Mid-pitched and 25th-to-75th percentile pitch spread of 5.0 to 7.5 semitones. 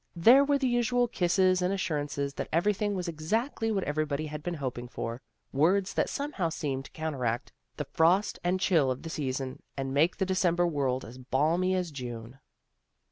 Yes: medium, 165 Hz; wide, 5.5 semitones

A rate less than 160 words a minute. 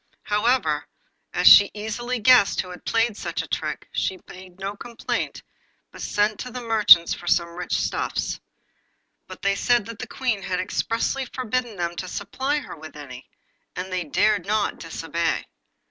No: average, 170 wpm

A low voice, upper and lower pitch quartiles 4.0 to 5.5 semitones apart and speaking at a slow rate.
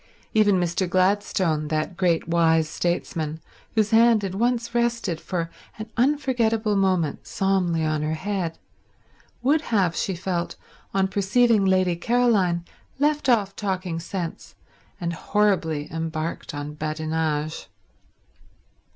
No: medium, 185 Hz; average, 4.6 semitones; slow, 115 wpm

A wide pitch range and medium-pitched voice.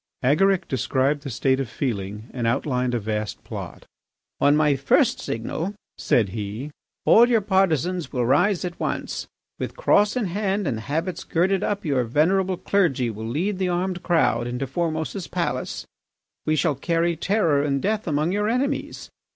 Yes: wide, 7.0 semitones; medium, 155 Hz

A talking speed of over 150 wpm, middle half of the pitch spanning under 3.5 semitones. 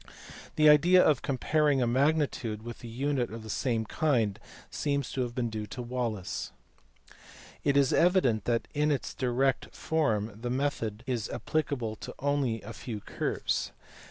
No: average, 160 wpm; average, 4.1 semitones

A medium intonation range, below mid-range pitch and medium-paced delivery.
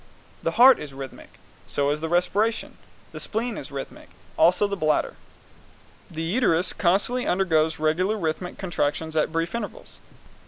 No: average, 4.7 semitones; medium, 170 Hz; average, 150 wpm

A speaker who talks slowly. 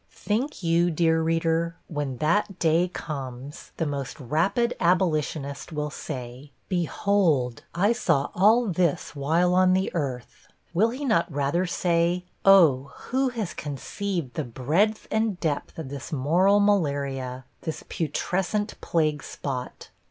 Yes: slow, 130 wpm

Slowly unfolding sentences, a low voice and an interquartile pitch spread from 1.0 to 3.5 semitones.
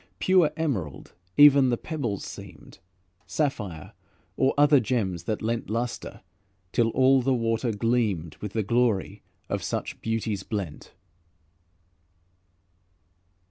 No: slow, 110 wpm; low, 115 Hz; average, 4.6 semitones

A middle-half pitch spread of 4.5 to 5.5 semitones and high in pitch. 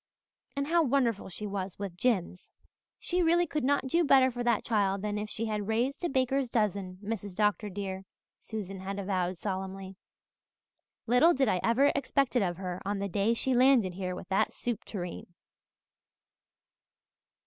Yes: average, 5.1 semitones; high, 210 Hz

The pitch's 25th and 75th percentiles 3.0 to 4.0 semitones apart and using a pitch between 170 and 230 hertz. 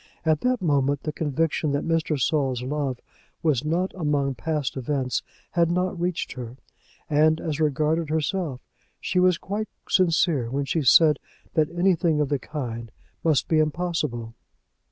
No: average, 3.4 semitones; medium, 155 Hz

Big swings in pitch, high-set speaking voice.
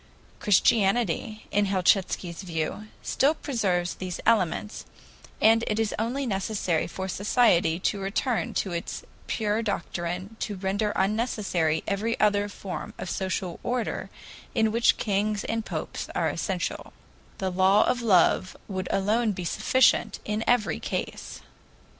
No: average, 3.0 semitones; high, 205 Hz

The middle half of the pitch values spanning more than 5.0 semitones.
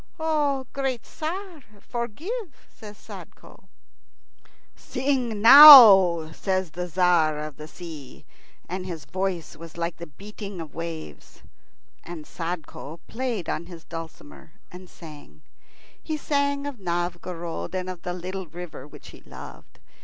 Yes: wide, 5.6 semitones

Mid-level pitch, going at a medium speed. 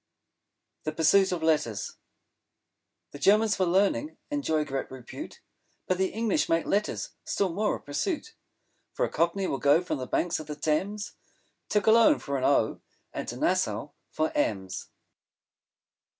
Yes: medium, 170 Hz; average, 150 wpm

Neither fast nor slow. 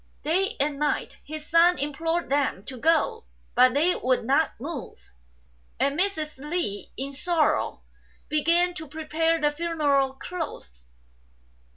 No: slow, 130 wpm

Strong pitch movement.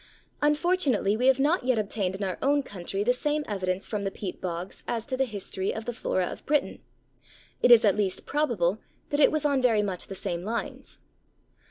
Yes: wide, 5.8 semitones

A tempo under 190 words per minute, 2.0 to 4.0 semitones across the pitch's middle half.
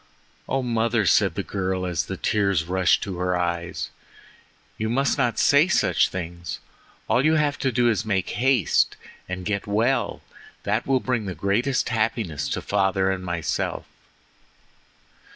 No: average, 150 wpm; average, 5.0 semitones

